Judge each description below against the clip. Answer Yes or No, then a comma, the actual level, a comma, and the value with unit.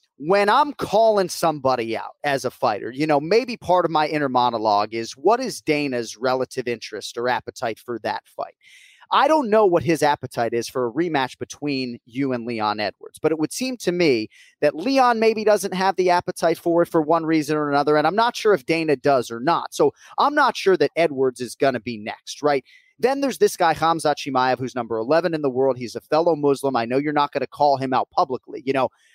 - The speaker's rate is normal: No, fast, 230 wpm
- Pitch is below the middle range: No, medium, 150 Hz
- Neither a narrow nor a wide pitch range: No, wide, 6.2 semitones